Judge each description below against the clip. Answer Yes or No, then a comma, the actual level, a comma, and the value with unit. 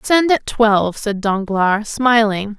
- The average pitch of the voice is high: Yes, high, 220 Hz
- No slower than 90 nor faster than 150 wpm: Yes, average, 140 wpm